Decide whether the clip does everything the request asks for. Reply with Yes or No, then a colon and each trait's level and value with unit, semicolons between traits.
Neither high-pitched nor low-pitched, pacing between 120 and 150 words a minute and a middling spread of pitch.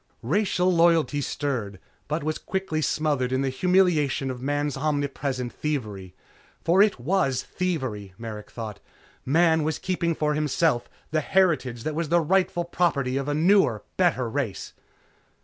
Yes: medium, 150 Hz; average, 145 wpm; average, 4.8 semitones